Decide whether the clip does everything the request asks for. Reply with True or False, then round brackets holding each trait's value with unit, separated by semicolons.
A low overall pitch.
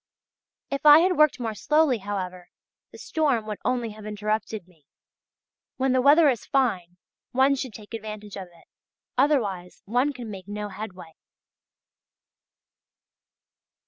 False (220 Hz)